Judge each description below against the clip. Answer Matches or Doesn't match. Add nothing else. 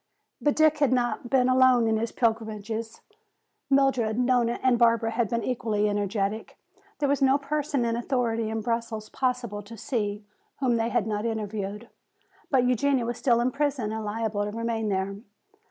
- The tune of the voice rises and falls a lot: Doesn't match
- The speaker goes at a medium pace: Matches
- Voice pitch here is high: Matches